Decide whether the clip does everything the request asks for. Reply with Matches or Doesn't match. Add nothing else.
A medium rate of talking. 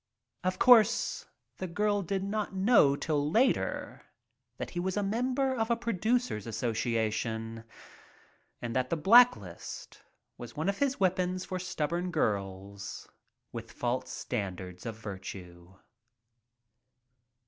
Doesn't match